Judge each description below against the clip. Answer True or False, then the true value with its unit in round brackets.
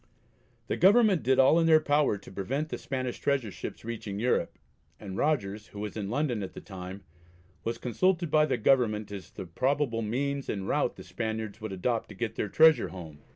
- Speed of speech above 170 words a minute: True (200 wpm)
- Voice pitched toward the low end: True (115 Hz)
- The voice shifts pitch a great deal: True (5.7 semitones)